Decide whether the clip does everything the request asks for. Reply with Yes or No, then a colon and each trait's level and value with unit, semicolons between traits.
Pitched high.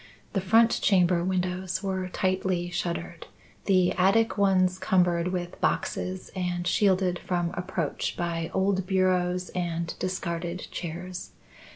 No: medium, 180 Hz